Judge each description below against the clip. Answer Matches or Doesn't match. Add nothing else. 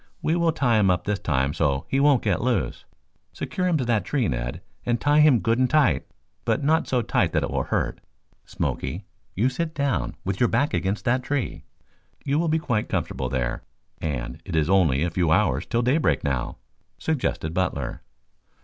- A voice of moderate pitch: Doesn't match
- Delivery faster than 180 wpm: Matches